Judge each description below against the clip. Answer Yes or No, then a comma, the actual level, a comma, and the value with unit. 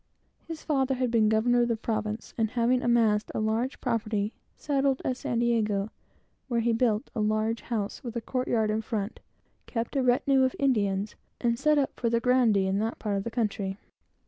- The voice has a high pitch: Yes, high, 230 Hz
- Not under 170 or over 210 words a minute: Yes, average, 200 wpm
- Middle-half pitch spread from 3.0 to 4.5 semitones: No, narrow, 2.6 semitones